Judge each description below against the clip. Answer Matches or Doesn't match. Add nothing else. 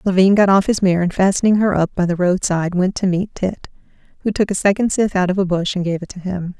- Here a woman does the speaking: Matches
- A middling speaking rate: Doesn't match